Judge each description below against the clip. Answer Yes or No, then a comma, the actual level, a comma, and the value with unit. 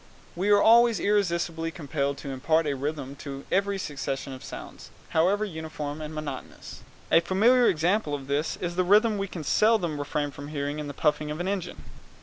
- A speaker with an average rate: Yes, average, 185 wpm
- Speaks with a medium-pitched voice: Yes, medium, 160 Hz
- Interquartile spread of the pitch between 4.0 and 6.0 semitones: Yes, average, 5.2 semitones